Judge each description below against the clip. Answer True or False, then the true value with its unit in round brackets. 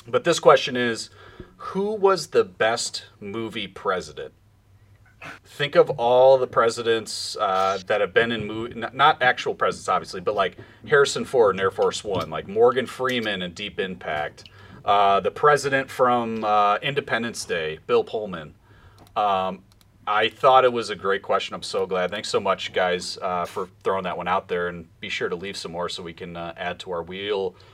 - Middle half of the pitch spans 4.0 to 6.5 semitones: True (5.1 semitones)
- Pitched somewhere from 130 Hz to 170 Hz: False (115 Hz)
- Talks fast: False (180 wpm)